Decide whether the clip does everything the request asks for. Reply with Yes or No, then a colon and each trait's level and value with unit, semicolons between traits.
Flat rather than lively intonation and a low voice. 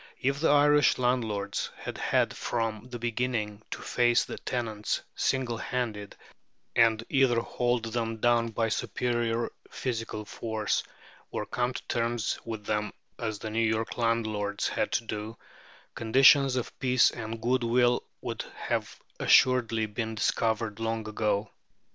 Yes: narrow, 2.0 semitones; low, 115 Hz